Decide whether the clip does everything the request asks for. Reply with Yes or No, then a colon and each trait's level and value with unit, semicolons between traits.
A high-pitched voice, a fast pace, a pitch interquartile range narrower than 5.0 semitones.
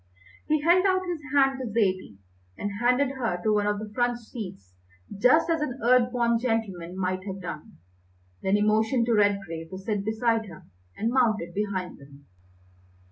No: high, 220 Hz; average, 175 wpm; average, 4.6 semitones